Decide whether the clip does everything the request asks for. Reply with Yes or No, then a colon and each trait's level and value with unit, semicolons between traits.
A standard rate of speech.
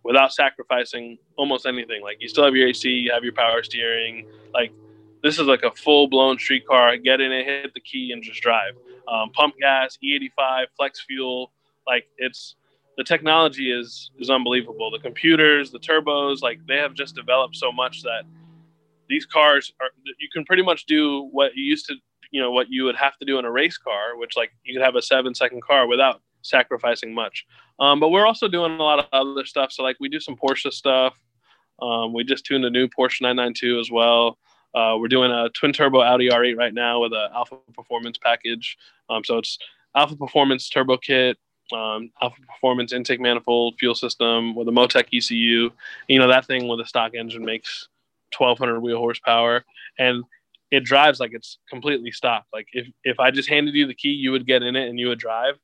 No: fast, 210 wpm